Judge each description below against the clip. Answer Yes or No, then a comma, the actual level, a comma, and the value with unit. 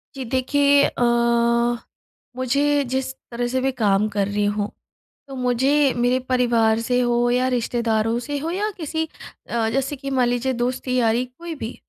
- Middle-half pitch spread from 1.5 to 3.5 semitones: Yes, narrow, 2.6 semitones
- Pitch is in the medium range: No, very high, 250 Hz